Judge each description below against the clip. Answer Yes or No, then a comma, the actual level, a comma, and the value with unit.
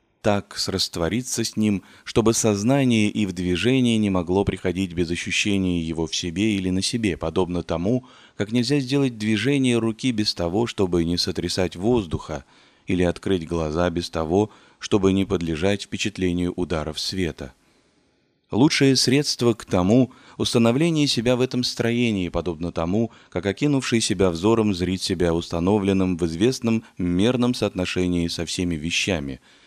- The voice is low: Yes, low, 100 Hz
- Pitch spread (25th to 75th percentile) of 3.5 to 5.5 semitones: Yes, average, 4.7 semitones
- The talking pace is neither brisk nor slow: Yes, average, 140 wpm